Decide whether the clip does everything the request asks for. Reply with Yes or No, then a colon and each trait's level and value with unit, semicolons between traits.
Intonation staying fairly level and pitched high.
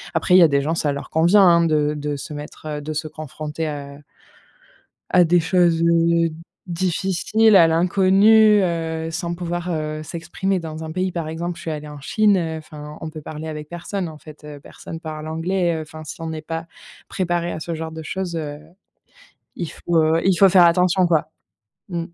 No: narrow, 2.1 semitones; medium, 165 Hz